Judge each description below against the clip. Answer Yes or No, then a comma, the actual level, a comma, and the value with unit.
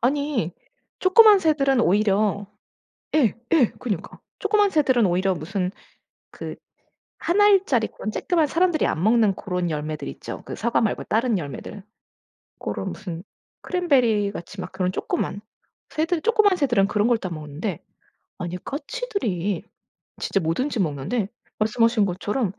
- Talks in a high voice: Yes, high, 220 Hz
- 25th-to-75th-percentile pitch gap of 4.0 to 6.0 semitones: No, wide, 8.0 semitones